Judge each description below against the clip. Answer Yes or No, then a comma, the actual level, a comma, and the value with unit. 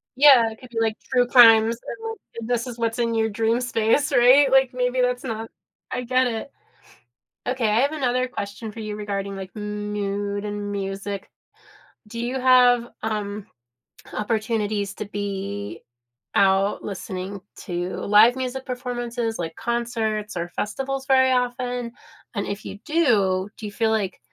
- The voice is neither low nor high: No, high, 225 Hz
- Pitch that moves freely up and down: No, average, 3.4 semitones